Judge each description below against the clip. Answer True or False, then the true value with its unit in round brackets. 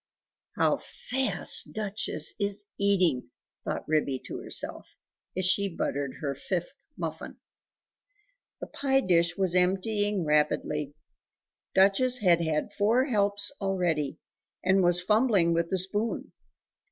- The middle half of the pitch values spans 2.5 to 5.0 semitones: True (3.6 semitones)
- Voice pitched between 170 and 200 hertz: True (190 Hz)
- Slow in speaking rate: True (115 wpm)